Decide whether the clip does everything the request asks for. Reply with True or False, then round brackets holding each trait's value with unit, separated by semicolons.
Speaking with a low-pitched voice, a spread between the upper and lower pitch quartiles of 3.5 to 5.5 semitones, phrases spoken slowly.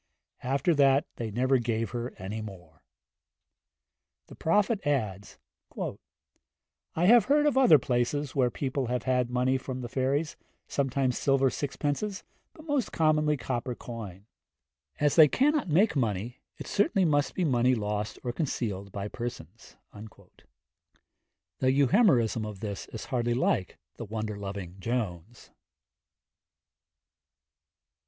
True (125 Hz; 4.9 semitones; 125 wpm)